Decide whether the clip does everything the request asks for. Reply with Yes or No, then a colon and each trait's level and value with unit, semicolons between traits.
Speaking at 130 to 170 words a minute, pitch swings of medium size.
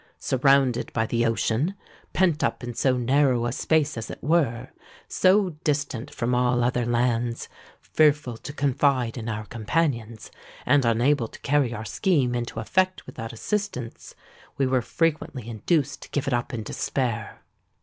Yes: average, 140 wpm; average, 3.8 semitones